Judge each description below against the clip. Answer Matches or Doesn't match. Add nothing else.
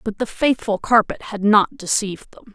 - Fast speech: Doesn't match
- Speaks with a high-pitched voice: Matches